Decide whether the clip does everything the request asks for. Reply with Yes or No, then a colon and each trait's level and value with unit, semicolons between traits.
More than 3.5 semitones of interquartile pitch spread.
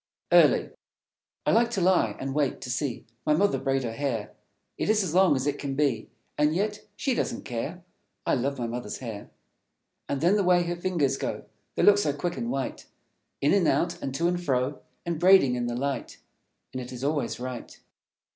Yes: wide, 5.5 semitones